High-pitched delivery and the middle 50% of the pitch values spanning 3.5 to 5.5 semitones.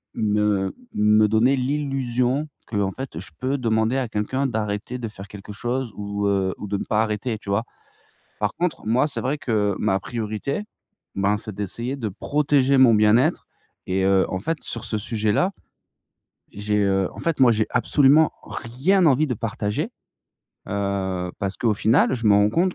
No: low, 110 Hz; average, 4.2 semitones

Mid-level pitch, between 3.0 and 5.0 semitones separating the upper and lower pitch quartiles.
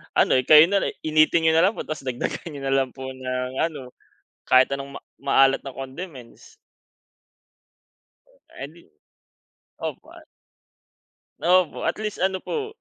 Yes: medium, 150 Hz; average, 4.7 semitones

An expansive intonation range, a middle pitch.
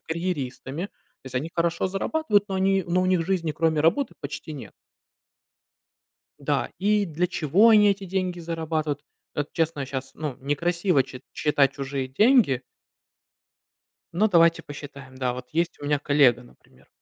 No: average, 4.8 semitones; medium, 165 Hz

